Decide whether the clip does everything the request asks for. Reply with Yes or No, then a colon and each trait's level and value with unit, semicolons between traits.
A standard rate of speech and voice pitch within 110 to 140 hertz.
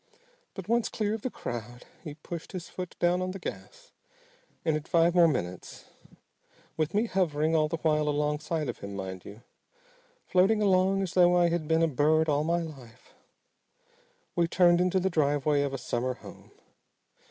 No: average, 175 wpm; medium, 160 Hz